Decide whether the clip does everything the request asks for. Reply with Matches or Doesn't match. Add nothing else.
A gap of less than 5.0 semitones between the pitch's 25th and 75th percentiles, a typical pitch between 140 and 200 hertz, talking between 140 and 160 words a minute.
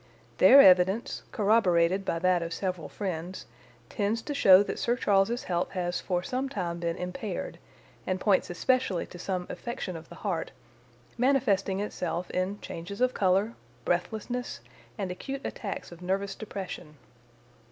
Matches